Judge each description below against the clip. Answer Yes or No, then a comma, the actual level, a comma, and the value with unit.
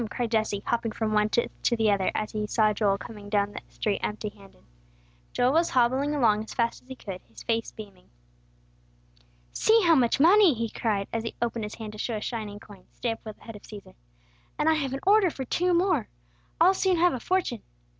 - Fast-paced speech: Yes, fast, 220 wpm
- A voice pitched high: Yes, high, 230 Hz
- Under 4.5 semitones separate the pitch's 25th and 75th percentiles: No, average, 4.8 semitones